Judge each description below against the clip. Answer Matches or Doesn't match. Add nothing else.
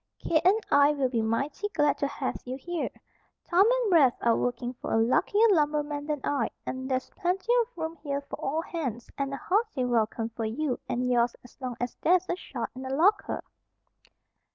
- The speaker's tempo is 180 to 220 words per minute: Matches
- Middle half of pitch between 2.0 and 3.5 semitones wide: Doesn't match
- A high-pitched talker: Matches